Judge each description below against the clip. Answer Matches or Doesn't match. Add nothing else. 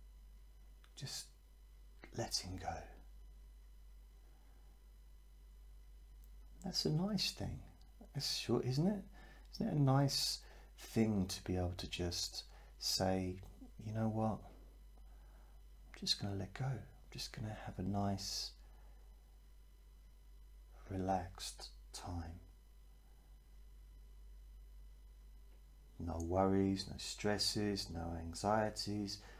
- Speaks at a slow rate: Matches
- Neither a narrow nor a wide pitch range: Doesn't match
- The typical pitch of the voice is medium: Doesn't match